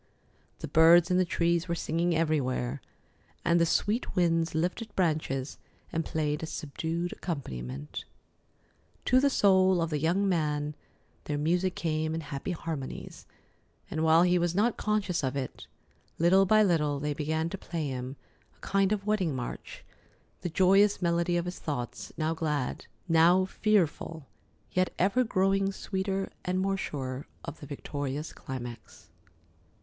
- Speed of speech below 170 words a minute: Yes, average, 150 wpm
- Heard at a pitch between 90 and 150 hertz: No, medium, 165 Hz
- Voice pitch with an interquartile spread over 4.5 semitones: No, average, 3.9 semitones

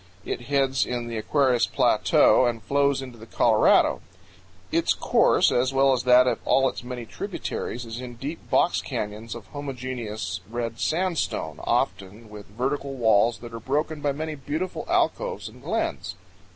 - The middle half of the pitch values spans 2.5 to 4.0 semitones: Yes, average, 3.3 semitones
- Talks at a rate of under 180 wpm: Yes, average, 160 wpm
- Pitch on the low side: Yes, low, 125 Hz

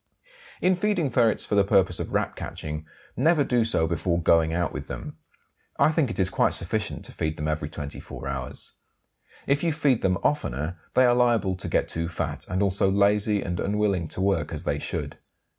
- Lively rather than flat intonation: Yes, wide, 6.3 semitones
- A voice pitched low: Yes, very low, 95 Hz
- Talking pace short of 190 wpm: No, average, 195 wpm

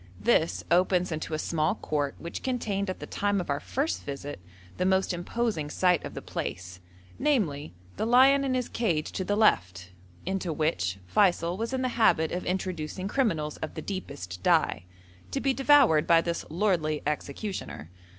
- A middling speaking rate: Yes, average, 170 wpm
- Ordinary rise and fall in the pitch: No, wide, 5.9 semitones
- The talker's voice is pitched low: No, medium, 180 Hz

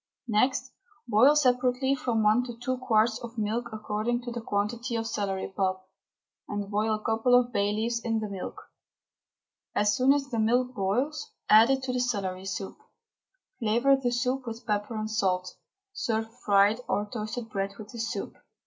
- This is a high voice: Yes, high, 225 Hz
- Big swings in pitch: No, average, 2.9 semitones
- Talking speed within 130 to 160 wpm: No, average, 175 wpm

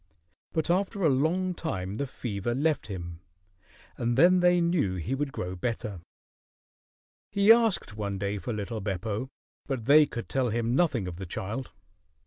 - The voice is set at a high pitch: No, low, 120 Hz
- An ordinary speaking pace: Yes, average, 160 wpm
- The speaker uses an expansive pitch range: Yes, wide, 8.1 semitones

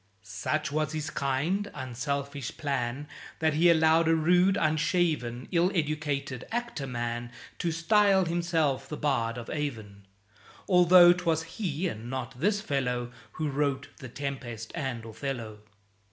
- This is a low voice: No, medium, 150 Hz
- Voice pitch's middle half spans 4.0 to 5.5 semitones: Yes, average, 4.9 semitones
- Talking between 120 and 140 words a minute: Yes, slow, 135 wpm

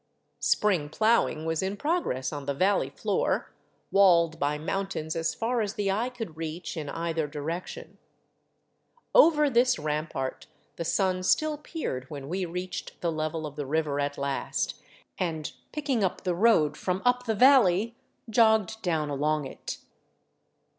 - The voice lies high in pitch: No, medium, 175 Hz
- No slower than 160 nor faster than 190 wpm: No, average, 150 wpm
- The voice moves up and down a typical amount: No, wide, 6.3 semitones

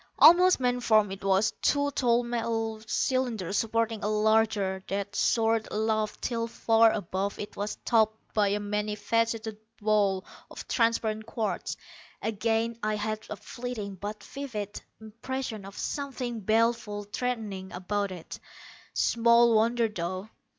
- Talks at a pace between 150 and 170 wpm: No, slow, 135 wpm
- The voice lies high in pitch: Yes, high, 220 Hz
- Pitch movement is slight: Yes, narrow, 2.1 semitones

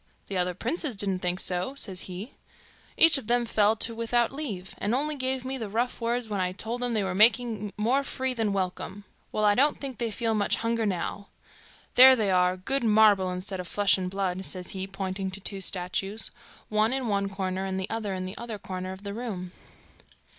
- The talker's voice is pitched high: Yes, high, 205 Hz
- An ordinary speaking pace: No, fast, 210 wpm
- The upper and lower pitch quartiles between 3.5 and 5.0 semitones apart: Yes, average, 3.9 semitones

